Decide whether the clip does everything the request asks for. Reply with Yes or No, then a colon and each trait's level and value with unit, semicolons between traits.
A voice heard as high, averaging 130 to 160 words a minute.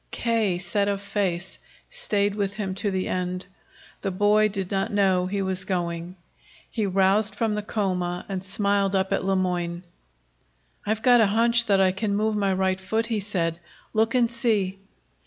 No: high, 195 Hz; average, 175 wpm